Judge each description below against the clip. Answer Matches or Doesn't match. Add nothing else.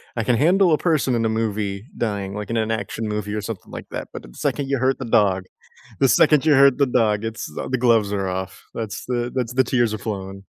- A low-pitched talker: Matches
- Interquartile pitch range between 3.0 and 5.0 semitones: Matches